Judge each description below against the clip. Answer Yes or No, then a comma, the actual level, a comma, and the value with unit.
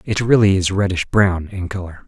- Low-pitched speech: Yes, very low, 95 Hz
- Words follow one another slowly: No, average, 200 wpm